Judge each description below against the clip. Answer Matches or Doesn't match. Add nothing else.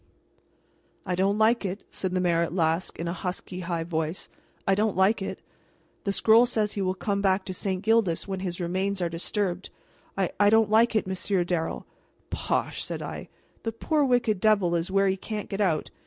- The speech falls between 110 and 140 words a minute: Doesn't match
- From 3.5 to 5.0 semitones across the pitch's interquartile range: Doesn't match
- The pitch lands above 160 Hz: Matches